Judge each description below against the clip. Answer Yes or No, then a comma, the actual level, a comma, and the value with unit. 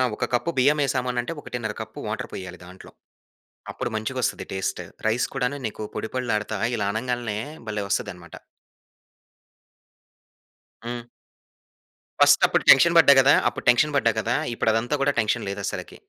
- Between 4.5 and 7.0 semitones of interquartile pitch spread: No, average, 2.9 semitones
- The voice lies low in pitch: Yes, low, 115 Hz